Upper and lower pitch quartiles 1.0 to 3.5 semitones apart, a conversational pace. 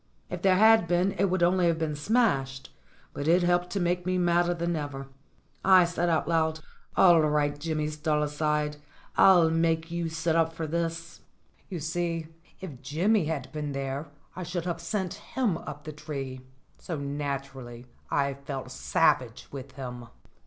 Yes: average, 3.2 semitones; average, 165 wpm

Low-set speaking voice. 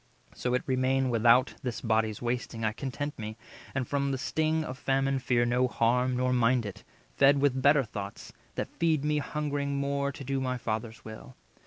Yes: low, 130 Hz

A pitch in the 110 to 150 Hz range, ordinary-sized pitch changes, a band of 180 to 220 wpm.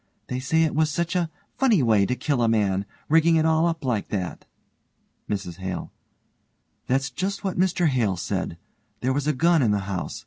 No: low, 135 Hz; wide, 7.9 semitones; average, 195 wpm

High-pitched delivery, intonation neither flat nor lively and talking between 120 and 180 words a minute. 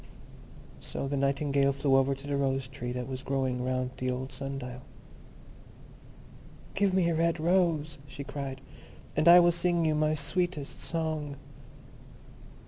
No: medium, 140 Hz; average, 3.3 semitones; average, 150 wpm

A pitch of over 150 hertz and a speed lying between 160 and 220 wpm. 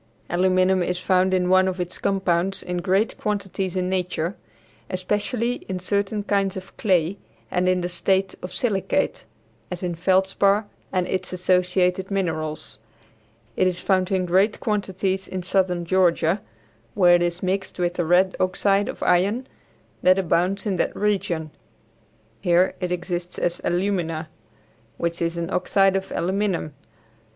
No: medium, 185 Hz; average, 145 wpm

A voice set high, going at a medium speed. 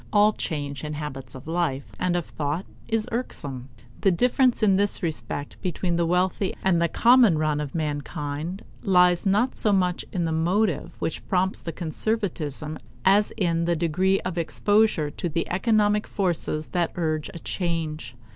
No: medium, 175 Hz; average, 165 wpm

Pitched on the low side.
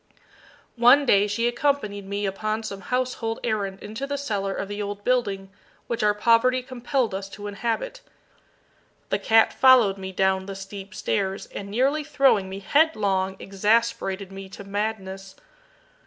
No: high, 205 Hz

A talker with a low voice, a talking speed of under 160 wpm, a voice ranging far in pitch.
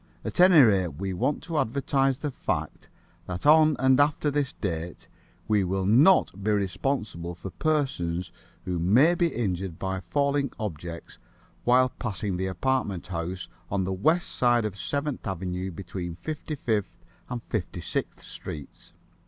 Yes: low, 105 Hz; average, 150 wpm; wide, 7.4 semitones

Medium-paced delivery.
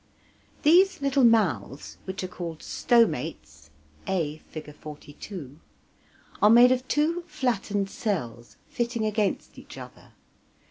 No: slow, 110 wpm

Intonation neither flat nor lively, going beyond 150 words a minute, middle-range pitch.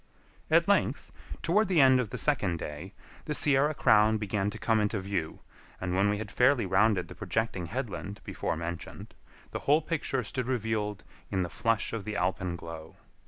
No: average, 5.0 semitones; average, 175 wpm; low, 105 Hz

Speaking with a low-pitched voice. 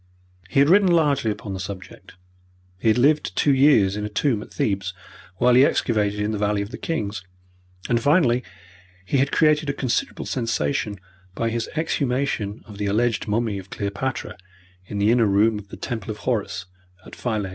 Yes: low, 115 Hz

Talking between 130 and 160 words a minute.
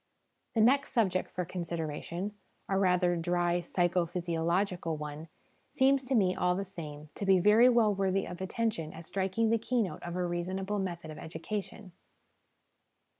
Yes: average, 155 wpm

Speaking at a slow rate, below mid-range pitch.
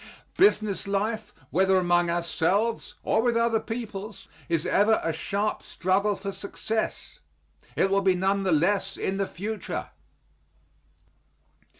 No: slow, 125 wpm; high, 195 Hz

